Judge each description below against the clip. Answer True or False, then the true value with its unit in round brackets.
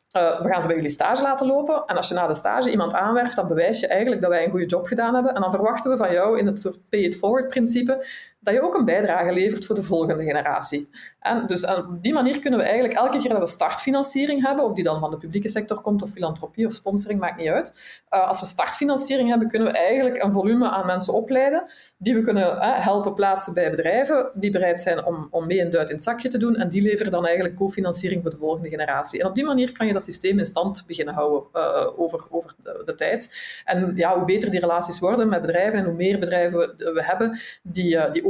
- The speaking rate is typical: False (250 wpm)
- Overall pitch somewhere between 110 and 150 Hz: False (195 Hz)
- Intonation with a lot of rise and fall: True (5.8 semitones)